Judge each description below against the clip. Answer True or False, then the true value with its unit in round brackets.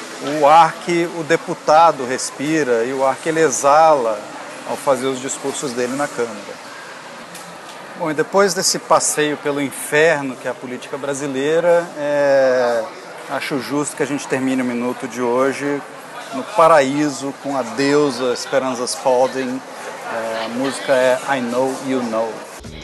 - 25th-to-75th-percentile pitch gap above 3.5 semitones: False (2.8 semitones)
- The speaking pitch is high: False (140 Hz)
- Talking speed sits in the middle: True (150 wpm)